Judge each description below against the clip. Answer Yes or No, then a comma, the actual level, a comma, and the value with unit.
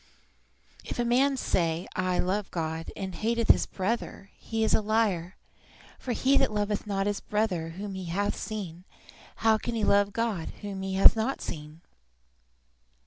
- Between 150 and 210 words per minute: Yes, average, 165 wpm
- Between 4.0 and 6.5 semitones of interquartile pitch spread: No, average, 3.4 semitones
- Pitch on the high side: Yes, high, 205 Hz